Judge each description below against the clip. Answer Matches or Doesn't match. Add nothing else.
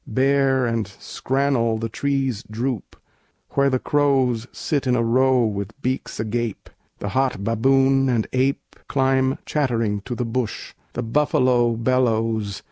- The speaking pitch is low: Matches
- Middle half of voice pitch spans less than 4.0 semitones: Matches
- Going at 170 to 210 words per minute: Doesn't match